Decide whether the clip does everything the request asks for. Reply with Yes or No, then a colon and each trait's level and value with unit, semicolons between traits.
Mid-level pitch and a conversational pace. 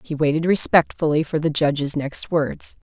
Yes: medium, 155 Hz; average, 165 wpm